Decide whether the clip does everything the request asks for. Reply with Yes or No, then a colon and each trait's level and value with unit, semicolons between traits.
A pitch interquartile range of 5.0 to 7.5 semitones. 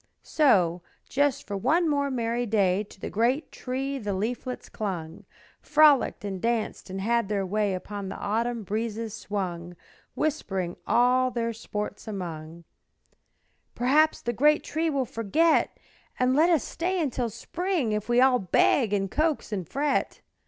Yes: average, 5.3 semitones